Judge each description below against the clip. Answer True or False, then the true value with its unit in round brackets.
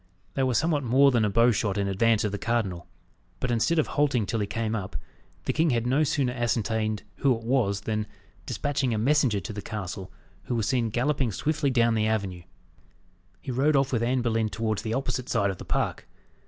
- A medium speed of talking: False (210 wpm)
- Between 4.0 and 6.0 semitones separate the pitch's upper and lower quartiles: False (3.5 semitones)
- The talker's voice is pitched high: False (115 Hz)